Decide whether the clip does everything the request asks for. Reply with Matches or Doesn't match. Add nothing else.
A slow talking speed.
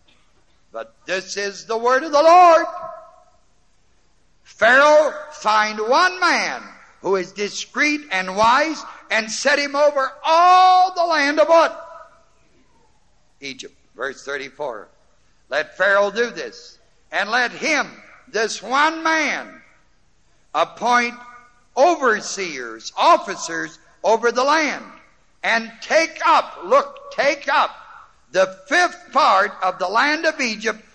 Matches